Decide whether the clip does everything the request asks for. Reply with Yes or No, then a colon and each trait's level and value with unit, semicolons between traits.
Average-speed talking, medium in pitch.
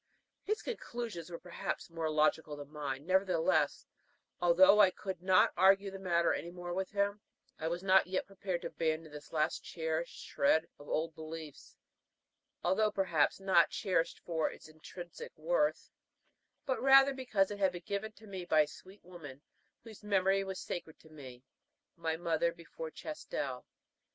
Yes: average, 165 wpm; medium, 175 Hz